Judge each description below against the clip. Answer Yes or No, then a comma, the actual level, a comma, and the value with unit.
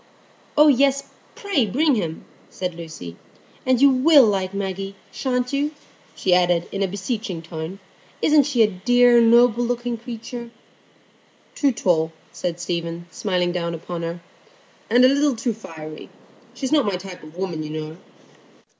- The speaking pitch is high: Yes, high, 200 Hz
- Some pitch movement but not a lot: No, wide, 6.4 semitones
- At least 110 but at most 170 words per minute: Yes, average, 155 wpm